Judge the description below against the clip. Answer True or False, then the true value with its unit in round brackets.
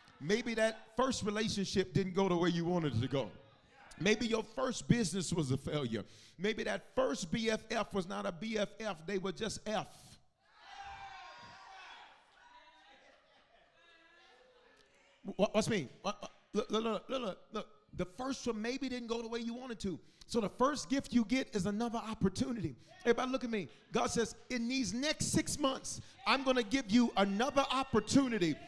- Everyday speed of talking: True (160 wpm)